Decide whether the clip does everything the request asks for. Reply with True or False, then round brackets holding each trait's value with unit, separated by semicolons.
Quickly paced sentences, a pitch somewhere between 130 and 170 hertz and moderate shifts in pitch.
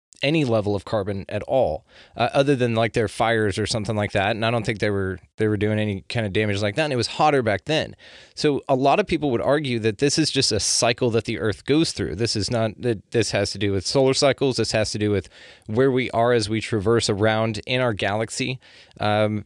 False (255 wpm; 110 Hz; 3.0 semitones)